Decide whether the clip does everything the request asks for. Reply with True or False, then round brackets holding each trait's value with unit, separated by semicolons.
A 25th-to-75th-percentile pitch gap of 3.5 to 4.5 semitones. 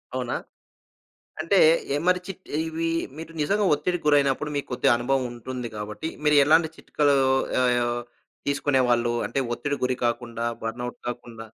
True (3.9 semitones)